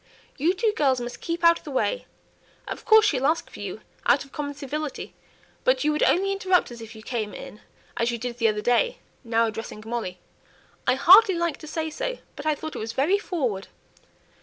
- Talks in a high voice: Yes, very high, 290 Hz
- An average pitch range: No, wide, 6.6 semitones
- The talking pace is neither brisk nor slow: No, fast, 210 wpm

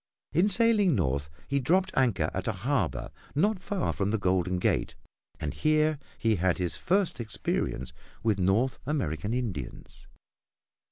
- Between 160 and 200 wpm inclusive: No, average, 145 wpm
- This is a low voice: Yes, low, 115 Hz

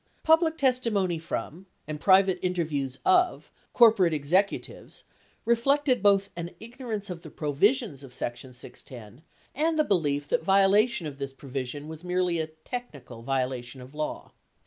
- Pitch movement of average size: No, wide, 7.8 semitones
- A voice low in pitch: No, medium, 175 Hz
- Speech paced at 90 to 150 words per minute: Yes, average, 145 wpm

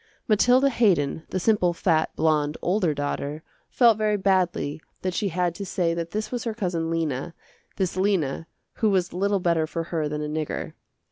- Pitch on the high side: No, medium, 175 Hz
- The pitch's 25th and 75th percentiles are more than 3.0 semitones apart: Yes, average, 4.2 semitones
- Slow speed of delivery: No, average, 180 wpm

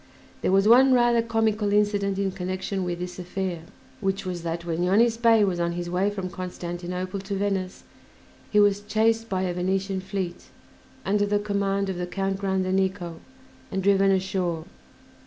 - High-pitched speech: Yes, high, 195 Hz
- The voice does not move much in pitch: Yes, narrow, 2.1 semitones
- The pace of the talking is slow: No, average, 165 wpm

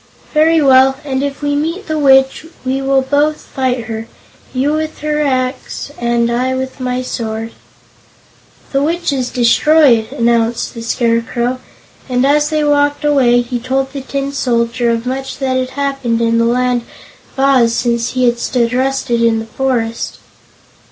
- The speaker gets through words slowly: No, average, 165 wpm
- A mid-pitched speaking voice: No, very high, 260 Hz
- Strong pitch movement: No, average, 2.8 semitones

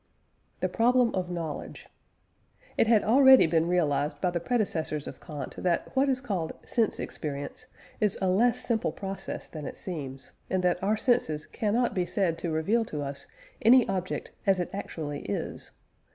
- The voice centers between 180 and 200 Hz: Yes, medium, 185 Hz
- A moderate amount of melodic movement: No, wide, 6.0 semitones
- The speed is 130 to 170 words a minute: Yes, average, 165 wpm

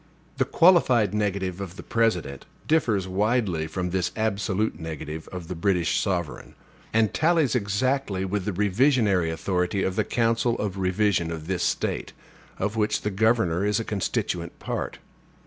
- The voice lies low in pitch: Yes, low, 100 Hz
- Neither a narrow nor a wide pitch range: Yes, average, 3.7 semitones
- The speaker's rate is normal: Yes, average, 150 wpm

